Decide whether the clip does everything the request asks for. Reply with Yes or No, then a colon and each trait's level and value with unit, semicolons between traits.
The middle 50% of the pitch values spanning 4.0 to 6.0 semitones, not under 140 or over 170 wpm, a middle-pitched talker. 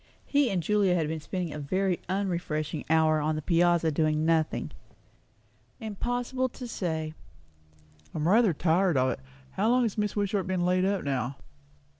Yes: average, 4.4 semitones; average, 160 wpm; medium, 175 Hz